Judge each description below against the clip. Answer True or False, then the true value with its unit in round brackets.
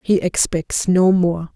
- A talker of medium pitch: True (175 Hz)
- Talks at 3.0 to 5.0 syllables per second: True (3.5 syllables/s)